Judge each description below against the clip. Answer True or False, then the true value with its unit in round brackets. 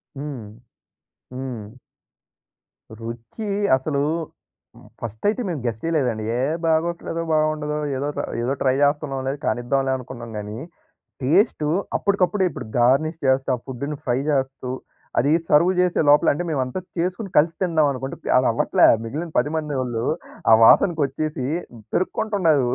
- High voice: False (140 Hz)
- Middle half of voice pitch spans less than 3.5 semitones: False (4.0 semitones)